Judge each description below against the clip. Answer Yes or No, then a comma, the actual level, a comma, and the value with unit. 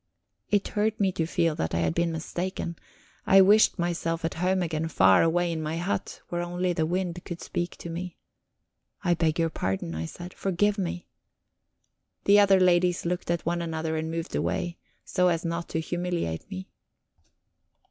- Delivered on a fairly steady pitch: Yes, narrow, 1.9 semitones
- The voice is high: No, medium, 170 Hz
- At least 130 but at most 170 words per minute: No, average, 180 wpm